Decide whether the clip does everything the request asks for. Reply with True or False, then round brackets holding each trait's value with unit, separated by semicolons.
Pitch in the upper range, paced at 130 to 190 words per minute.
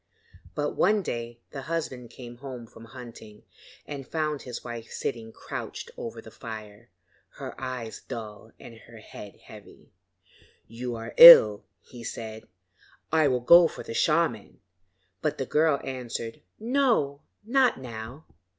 False (125 Hz; 140 wpm)